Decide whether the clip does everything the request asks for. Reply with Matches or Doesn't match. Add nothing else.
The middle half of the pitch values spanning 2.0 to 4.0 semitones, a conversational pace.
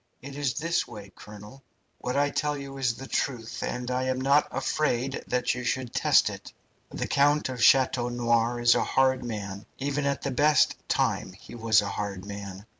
Matches